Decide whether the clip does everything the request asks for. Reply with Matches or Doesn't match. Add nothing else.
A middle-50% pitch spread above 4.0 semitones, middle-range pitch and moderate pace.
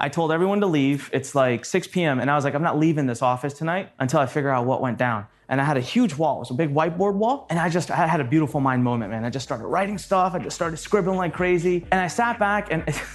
Doesn't match